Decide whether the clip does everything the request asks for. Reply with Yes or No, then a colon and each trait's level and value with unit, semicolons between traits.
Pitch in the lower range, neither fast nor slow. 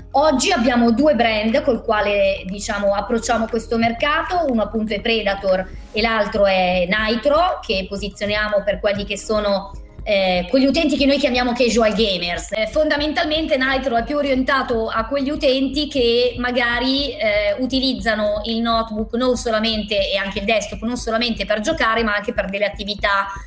No: high, 230 Hz; average, 155 wpm